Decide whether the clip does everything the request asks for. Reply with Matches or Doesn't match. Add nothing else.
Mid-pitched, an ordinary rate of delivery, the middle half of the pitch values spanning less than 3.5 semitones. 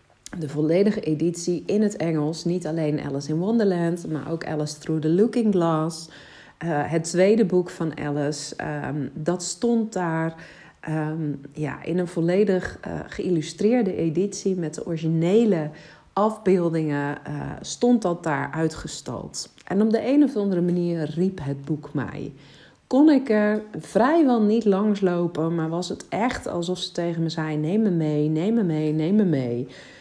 Doesn't match